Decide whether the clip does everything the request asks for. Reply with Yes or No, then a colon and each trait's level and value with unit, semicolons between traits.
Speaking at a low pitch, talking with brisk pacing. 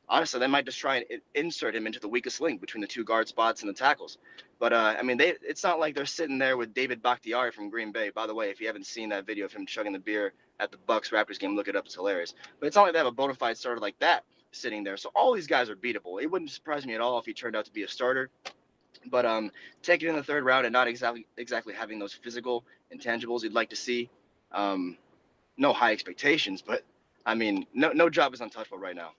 Yes: low, 125 Hz; fast, 265 wpm